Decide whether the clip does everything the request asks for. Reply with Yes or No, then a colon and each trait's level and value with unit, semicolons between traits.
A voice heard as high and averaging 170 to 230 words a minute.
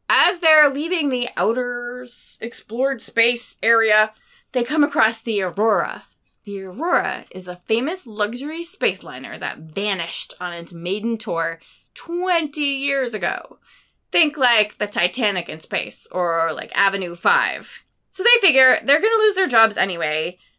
No: high, 230 Hz; average, 145 wpm